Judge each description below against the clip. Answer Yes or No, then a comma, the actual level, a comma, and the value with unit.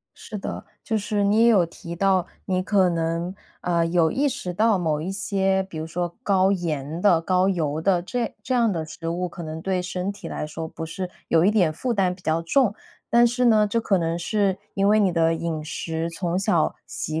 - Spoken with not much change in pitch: No, average, 3.4 semitones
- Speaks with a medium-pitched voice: Yes, medium, 180 Hz